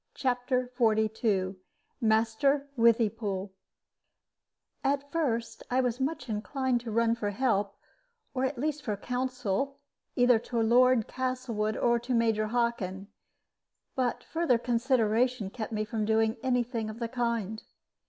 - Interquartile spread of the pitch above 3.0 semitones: No, average, 2.7 semitones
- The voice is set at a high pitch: Yes, high, 235 Hz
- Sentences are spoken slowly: Yes, slow, 130 wpm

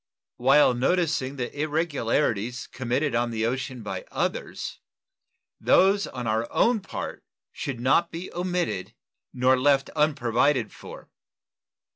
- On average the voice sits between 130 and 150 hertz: Yes, low, 135 Hz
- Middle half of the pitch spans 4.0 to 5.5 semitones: Yes, average, 4.3 semitones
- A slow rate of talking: Yes, slow, 115 wpm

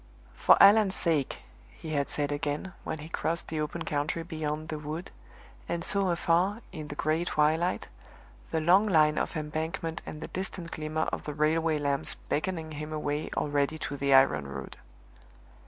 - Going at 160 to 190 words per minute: Yes, average, 170 wpm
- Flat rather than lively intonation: Yes, narrow, 2.1 semitones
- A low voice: No, medium, 155 Hz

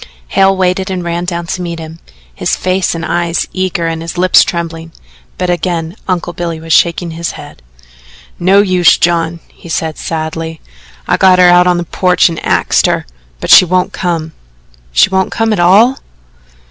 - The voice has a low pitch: No, medium, 175 Hz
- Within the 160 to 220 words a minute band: Yes, average, 180 wpm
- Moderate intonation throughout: No, narrow, 1.8 semitones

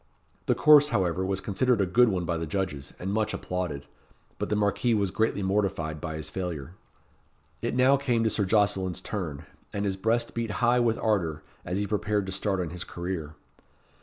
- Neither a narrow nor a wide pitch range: Yes, average, 3.8 semitones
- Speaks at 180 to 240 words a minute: Yes, average, 190 wpm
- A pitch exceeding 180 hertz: No, very low, 95 Hz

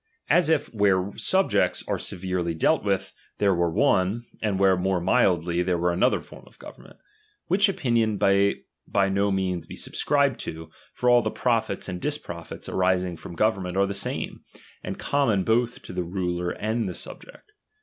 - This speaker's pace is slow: No, average, 170 wpm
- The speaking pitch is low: Yes, very low, 95 Hz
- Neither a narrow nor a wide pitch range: Yes, average, 4.0 semitones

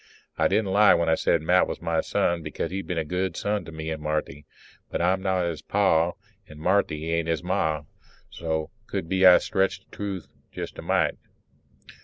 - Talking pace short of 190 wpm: No, average, 200 wpm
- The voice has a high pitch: No, very low, 85 Hz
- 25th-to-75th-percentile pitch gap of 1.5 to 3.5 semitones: Yes, average, 3.0 semitones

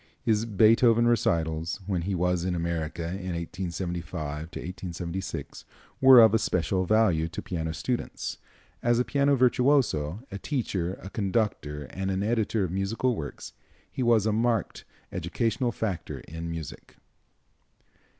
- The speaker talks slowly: Yes, slow, 130 wpm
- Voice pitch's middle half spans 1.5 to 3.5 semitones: No, average, 5.3 semitones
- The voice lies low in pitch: Yes, very low, 95 Hz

